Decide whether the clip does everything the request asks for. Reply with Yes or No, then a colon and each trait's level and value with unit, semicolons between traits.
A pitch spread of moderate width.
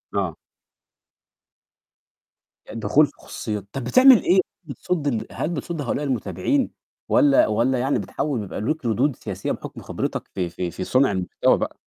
No: wide, 6.6 semitones